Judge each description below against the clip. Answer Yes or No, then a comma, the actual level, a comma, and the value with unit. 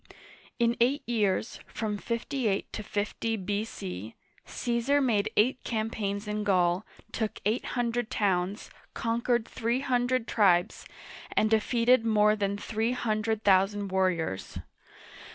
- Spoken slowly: Yes, slow, 130 wpm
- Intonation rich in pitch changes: No, average, 2.7 semitones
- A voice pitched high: Yes, high, 215 Hz